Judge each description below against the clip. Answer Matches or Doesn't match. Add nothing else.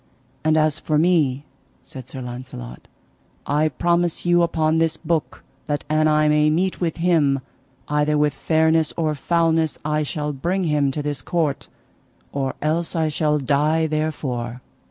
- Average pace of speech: Matches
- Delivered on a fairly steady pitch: Matches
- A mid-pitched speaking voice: Matches